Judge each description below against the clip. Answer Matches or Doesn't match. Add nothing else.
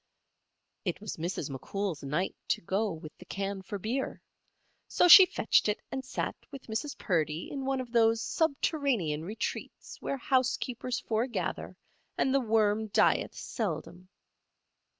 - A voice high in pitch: Matches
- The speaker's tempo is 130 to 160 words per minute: Matches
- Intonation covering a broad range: Matches